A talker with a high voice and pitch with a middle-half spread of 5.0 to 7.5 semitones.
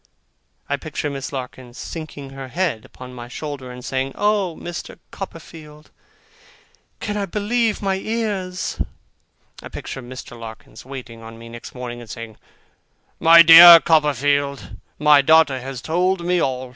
No: medium, 145 Hz; wide, 5.4 semitones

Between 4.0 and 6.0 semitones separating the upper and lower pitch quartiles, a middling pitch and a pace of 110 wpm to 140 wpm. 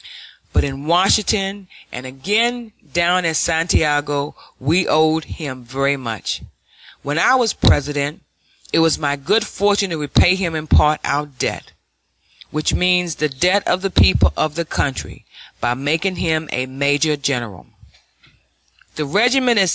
Yes: average, 4.3 semitones; medium, 155 Hz; slow, 135 wpm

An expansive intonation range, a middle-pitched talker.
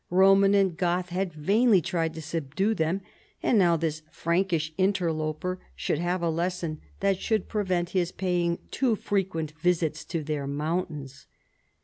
No: average, 3.2 semitones; medium, 175 Hz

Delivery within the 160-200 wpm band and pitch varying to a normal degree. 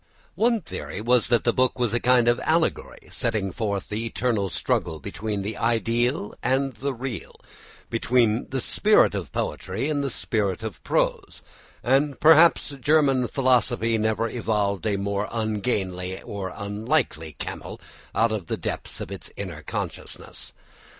No: average, 150 wpm; average, 4.1 semitones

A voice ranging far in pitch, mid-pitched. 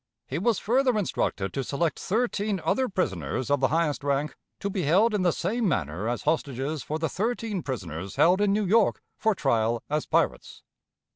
Yes: wide, 7.6 semitones; medium, 165 Hz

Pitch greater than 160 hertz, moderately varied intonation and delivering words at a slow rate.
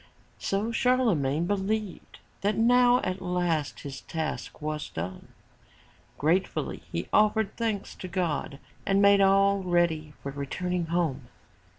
Yes: medium, 185 Hz; average, 4.6 semitones; slow, 120 wpm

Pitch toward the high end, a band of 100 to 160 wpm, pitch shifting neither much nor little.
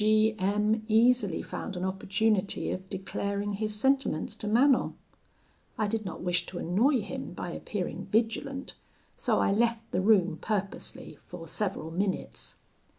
Yes: high, 210 Hz; average, 145 wpm; average, 3.0 semitones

